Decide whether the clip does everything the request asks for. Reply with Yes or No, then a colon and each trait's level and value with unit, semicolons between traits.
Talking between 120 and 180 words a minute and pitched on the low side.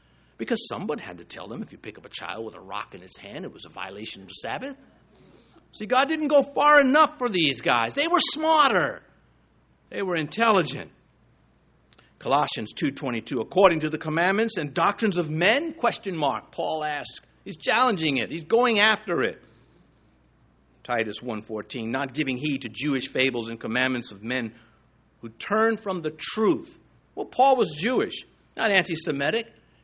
No: average, 175 wpm; medium, 165 Hz